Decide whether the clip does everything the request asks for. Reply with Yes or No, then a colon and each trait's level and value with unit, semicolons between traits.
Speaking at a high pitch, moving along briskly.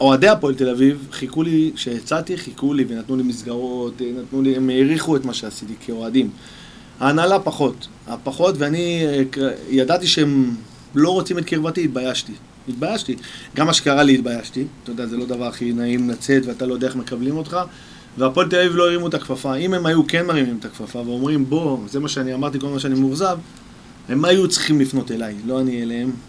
No: low, 135 Hz; fast, 185 wpm